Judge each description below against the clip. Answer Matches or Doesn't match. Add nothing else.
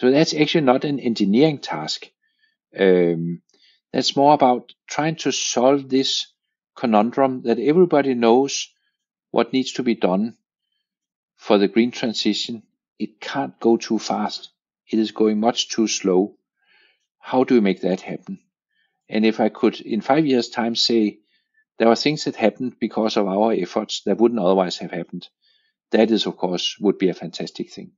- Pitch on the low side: Matches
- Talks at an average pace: Matches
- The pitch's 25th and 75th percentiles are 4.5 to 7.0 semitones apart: Matches